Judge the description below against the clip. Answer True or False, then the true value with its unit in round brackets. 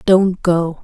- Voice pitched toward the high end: False (180 Hz)